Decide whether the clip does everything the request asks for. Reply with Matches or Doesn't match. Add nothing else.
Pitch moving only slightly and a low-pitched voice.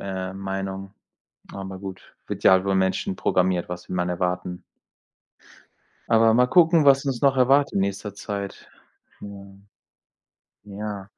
Doesn't match